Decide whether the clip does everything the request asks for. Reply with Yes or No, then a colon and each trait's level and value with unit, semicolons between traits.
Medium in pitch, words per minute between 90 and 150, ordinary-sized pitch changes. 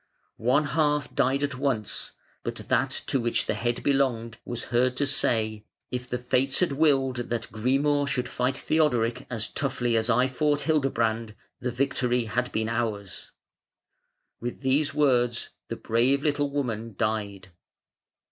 No: low, 125 Hz; average, 145 wpm; average, 3.3 semitones